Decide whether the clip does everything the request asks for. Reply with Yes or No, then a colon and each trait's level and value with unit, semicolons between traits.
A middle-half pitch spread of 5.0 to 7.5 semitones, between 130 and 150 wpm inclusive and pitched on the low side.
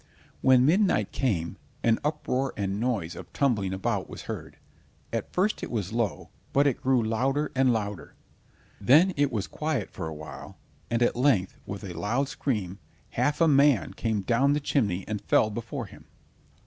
No: wide, 5.5 semitones; average, 175 wpm; low, 120 Hz